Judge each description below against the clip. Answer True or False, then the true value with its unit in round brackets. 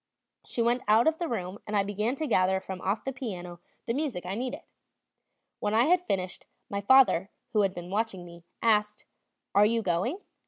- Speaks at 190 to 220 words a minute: True (195 wpm)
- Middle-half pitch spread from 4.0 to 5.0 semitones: True (4.5 semitones)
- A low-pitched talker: False (210 Hz)